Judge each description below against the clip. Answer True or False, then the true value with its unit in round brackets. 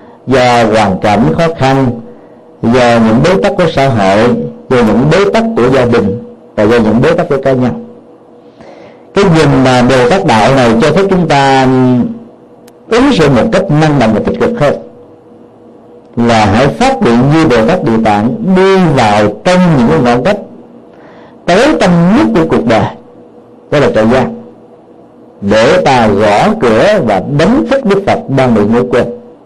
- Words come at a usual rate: True (175 wpm)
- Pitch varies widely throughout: True (7.3 semitones)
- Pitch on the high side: False (135 Hz)